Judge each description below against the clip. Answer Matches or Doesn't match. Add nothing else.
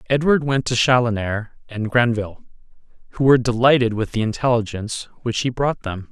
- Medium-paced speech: Matches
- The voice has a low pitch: Matches